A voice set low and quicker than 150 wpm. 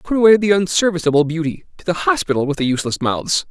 No: medium, 170 Hz; fast, 205 wpm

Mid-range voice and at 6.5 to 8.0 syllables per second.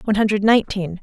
No: high, 205 Hz; 7.7 syllables/s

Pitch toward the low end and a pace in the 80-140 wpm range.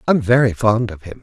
No: low, 110 Hz; fast, 245 wpm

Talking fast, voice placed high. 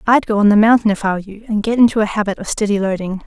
Yes: fast, 315 wpm; high, 210 Hz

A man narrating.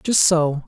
Yes: male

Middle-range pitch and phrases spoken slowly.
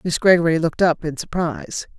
No: medium, 165 Hz; average, 180 wpm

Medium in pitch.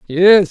Yes: medium, 180 Hz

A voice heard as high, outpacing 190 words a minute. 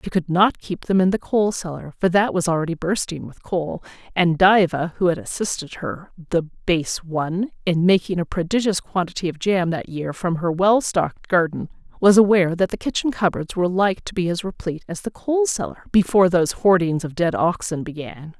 No: medium, 180 Hz; average, 200 wpm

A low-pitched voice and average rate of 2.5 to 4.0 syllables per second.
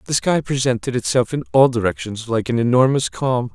No: low, 125 Hz; 5.4 syllables/s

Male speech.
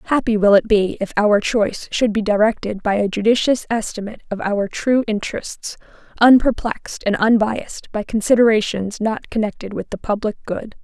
No: female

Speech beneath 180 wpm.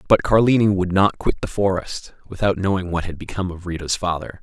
No: fast, 205 wpm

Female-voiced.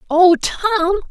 Yes: female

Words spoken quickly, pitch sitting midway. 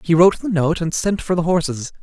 Yes: fast, 265 wpm; medium, 170 Hz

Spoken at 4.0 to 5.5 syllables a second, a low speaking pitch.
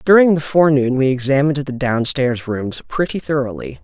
Yes: 5.4 syllables/s; low, 130 Hz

